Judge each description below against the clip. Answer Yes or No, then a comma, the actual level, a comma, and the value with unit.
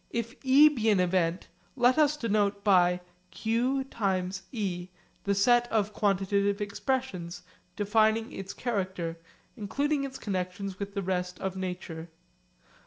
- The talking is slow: Yes, slow, 120 wpm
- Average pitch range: Yes, average, 4.0 semitones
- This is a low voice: No, high, 200 Hz